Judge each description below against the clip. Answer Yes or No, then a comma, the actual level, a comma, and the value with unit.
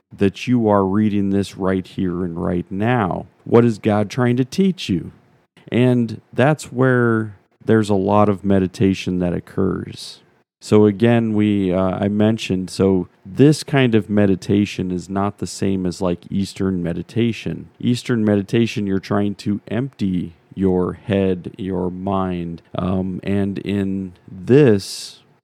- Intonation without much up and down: No, average, 3.4 semitones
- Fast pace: No, average, 140 wpm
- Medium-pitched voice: No, low, 100 Hz